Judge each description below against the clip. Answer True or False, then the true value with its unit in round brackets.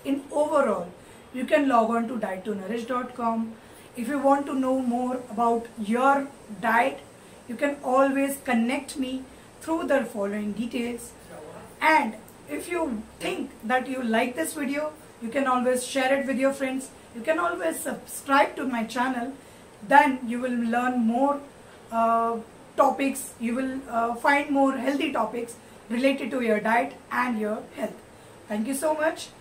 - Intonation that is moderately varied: True (3.0 semitones)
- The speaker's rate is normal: True (155 wpm)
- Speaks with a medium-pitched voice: False (255 Hz)